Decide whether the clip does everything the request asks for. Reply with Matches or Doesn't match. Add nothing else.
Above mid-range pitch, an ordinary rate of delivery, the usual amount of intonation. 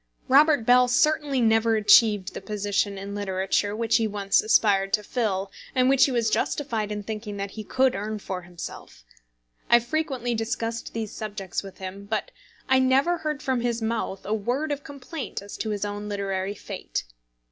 Matches